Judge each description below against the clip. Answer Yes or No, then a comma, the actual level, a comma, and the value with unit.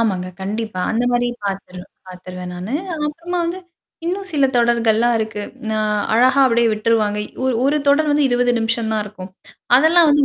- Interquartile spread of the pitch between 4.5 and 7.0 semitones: Yes, average, 5.0 semitones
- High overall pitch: Yes, high, 230 Hz